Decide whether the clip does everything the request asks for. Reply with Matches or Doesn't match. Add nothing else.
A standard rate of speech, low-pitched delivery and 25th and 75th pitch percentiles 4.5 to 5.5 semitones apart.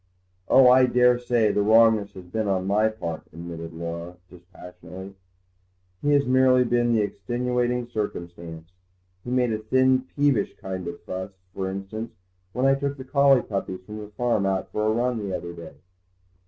Matches